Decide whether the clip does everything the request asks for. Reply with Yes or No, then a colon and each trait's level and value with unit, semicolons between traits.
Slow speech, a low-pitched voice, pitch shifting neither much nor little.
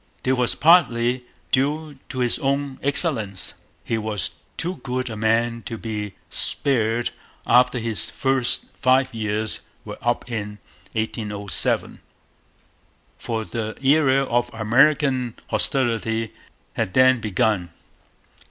Yes: slow, 115 wpm; low, 120 Hz; average, 3.2 semitones